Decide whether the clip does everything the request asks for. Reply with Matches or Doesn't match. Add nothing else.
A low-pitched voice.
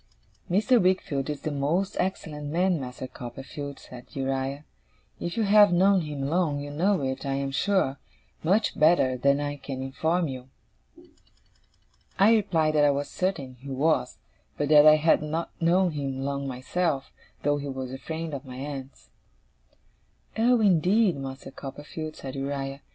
Doesn't match